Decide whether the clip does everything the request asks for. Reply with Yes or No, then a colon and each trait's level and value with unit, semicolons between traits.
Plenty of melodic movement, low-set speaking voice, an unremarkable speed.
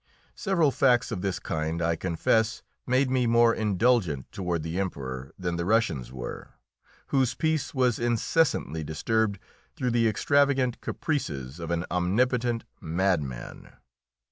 No: wide, 7.0 semitones; low, 105 Hz; slow, 130 wpm